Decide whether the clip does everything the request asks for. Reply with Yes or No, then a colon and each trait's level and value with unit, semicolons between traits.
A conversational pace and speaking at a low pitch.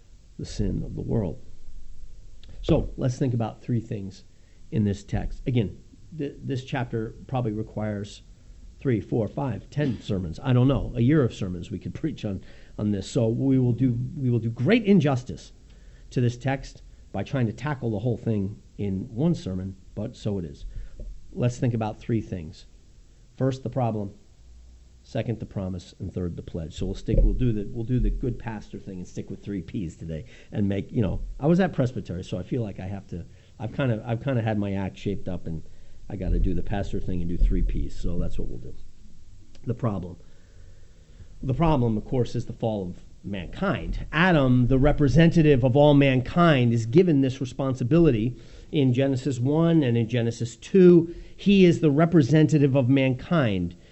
Yes: average, 195 wpm; low, 115 Hz